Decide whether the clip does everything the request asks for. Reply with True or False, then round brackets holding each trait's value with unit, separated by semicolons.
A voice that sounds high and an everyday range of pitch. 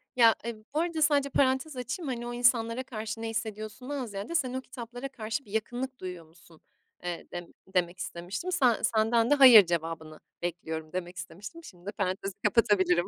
False (225 Hz; 5.9 semitones)